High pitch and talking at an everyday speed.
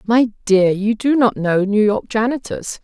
Yes: high, 220 Hz; average, 190 wpm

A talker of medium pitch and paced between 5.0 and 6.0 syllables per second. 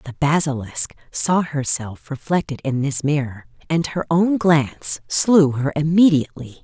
No: medium, 150 Hz; 4.4 syllables/s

